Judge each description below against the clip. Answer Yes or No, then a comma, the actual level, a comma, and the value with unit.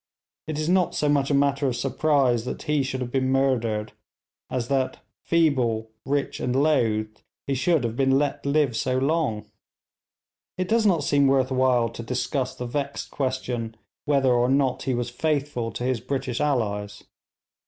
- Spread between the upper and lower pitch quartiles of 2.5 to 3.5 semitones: Yes, average, 2.8 semitones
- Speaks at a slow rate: No, average, 170 wpm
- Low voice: Yes, low, 130 Hz